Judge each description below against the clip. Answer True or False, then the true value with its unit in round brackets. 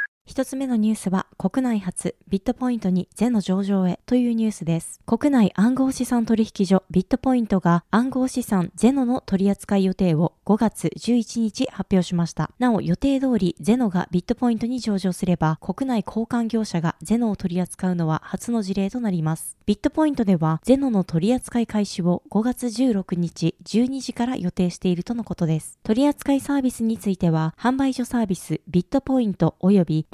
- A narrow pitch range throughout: False (5.1 semitones)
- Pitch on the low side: False (210 Hz)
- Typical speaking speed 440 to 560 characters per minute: False (365 characters per minute)